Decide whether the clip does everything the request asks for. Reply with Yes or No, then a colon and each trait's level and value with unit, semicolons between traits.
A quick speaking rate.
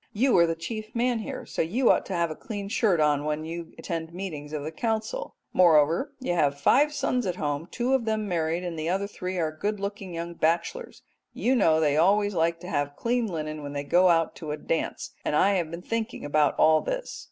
Yes: fast, 230 wpm